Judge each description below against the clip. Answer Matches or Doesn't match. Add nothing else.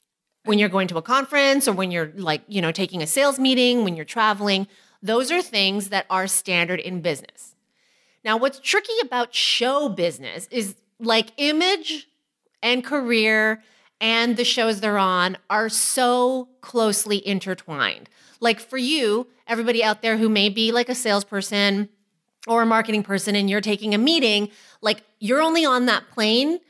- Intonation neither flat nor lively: Matches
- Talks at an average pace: Matches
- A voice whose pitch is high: Matches